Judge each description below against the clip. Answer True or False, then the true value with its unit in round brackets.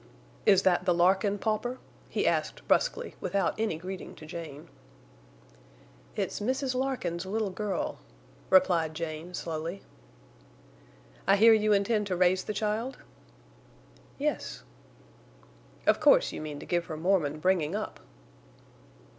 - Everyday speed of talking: False (125 wpm)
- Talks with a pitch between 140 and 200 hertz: True (190 Hz)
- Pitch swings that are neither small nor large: True (4.0 semitones)